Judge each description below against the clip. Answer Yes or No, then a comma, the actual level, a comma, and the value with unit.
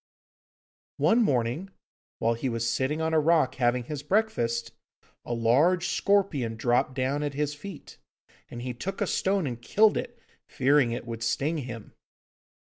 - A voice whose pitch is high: No, low, 135 Hz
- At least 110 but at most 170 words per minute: Yes, average, 155 wpm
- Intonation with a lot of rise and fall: Yes, wide, 5.7 semitones